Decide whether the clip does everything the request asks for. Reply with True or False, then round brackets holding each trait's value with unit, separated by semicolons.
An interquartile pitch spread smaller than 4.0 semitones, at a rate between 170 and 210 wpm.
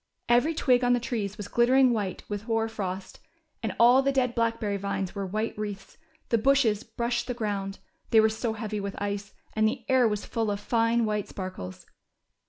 True (2.8 semitones; 190 wpm)